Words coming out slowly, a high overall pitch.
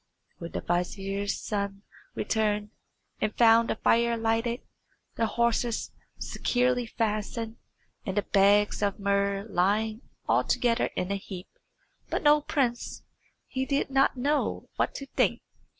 Yes: slow, 130 wpm; high, 220 Hz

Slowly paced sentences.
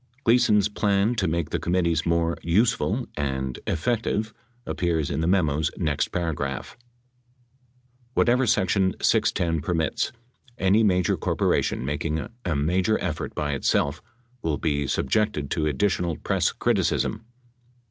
Yes: slow, 125 wpm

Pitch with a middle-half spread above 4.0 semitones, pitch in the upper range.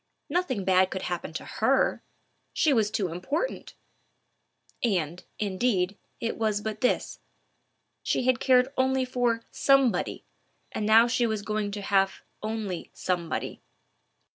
Yes: average, 4.6 semitones; high, 215 Hz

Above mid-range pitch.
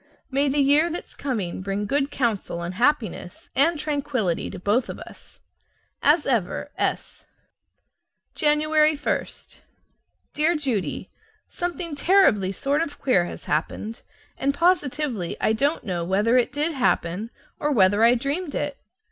Yes: very high, 275 Hz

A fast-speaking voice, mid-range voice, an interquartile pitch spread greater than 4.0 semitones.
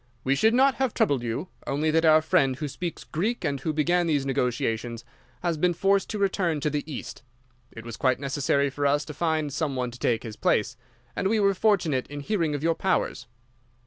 Yes: fast, 210 wpm; medium, 150 Hz; average, 4.7 semitones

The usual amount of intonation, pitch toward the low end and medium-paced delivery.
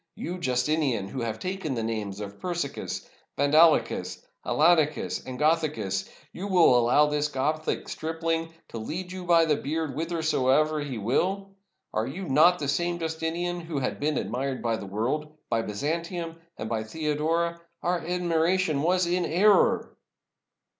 No: average, 4.6 semitones; medium, 155 Hz; average, 155 wpm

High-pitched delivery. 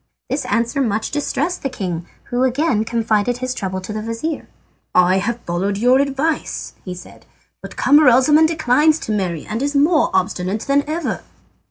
Yes: high, 245 Hz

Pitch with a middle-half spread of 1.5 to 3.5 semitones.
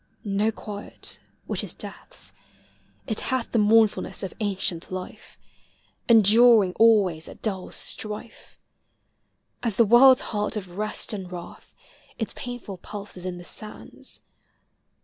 Yes: average, 3.2 semitones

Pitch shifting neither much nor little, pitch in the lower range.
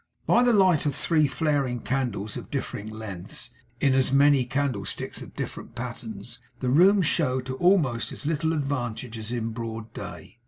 Yes: average, 4.4 semitones; low, 130 Hz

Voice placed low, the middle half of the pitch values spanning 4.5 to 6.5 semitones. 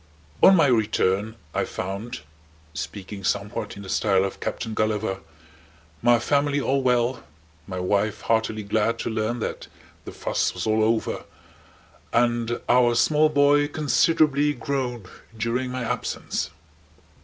No: low, 115 Hz; average, 3.7 semitones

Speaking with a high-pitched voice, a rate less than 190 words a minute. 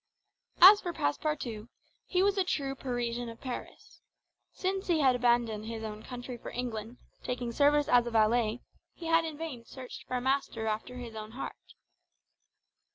Yes: high, 245 Hz; average, 165 wpm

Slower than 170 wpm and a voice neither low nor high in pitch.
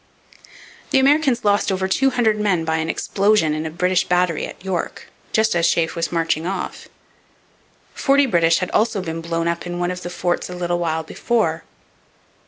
No: average, 185 wpm; medium, 180 Hz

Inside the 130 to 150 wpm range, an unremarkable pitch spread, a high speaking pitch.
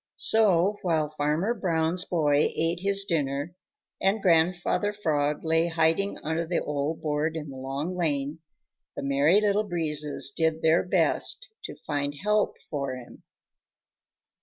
No: slow, 135 wpm; average, 3.6 semitones; medium, 160 Hz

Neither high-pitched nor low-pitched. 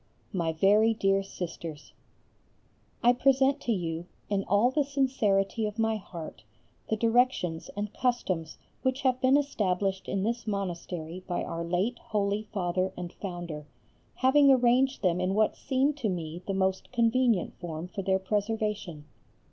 No: high, 200 Hz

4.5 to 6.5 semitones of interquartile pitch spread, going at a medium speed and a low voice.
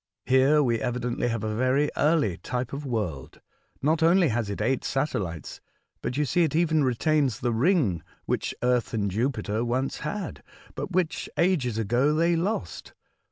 Yes: average, 5.3 semitones; average, 160 wpm; low, 130 Hz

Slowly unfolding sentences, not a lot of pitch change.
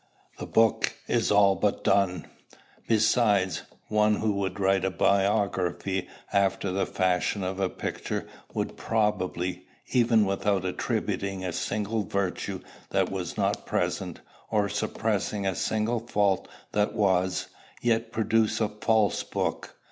Yes: slow, 130 wpm; narrow, 2.3 semitones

